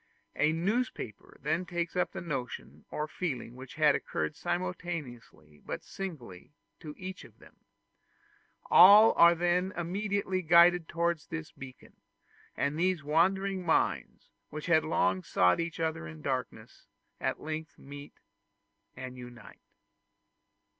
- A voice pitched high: No, medium, 160 Hz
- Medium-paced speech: No, slow, 130 wpm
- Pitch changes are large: No, average, 4.3 semitones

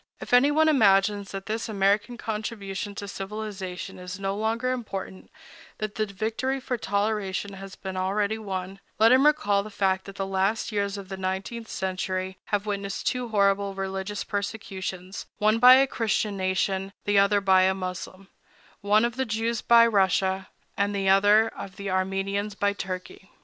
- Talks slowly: No, average, 160 wpm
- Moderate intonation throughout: No, narrow, 2.2 semitones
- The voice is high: Yes, high, 200 Hz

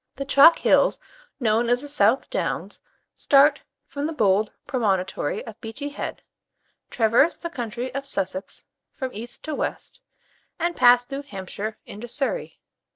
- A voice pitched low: No, high, 245 Hz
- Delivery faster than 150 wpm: No, average, 145 wpm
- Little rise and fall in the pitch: No, average, 4.7 semitones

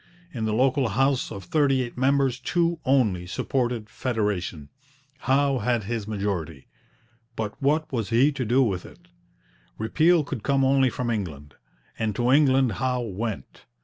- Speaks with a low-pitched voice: Yes, low, 120 Hz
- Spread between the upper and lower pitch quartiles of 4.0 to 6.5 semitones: Yes, average, 4.3 semitones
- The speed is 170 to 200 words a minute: No, average, 150 wpm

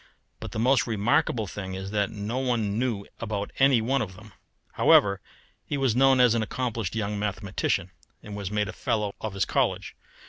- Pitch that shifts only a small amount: No, average, 3.1 semitones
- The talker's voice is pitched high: No, low, 110 Hz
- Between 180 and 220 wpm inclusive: Yes, average, 185 wpm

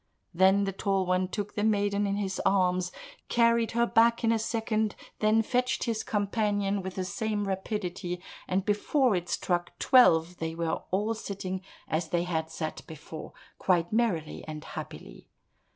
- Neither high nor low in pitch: No, high, 195 Hz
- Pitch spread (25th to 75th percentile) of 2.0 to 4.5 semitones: Yes, average, 3.5 semitones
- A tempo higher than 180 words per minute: No, average, 160 wpm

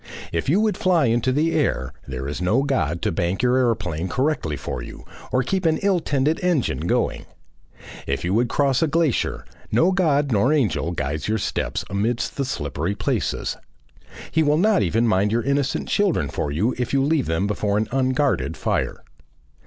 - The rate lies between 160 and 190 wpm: Yes, average, 185 wpm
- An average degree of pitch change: No, wide, 8.3 semitones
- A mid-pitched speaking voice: No, low, 125 Hz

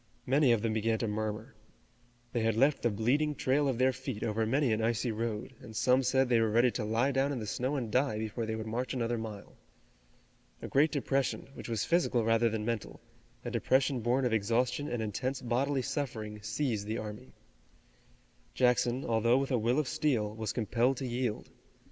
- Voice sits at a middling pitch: No, low, 120 Hz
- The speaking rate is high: No, average, 195 wpm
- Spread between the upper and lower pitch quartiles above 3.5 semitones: No, average, 3.1 semitones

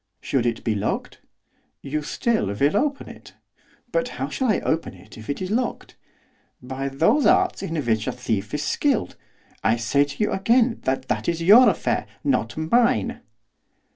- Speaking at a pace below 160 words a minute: No, average, 170 wpm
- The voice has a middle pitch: Yes, medium, 150 Hz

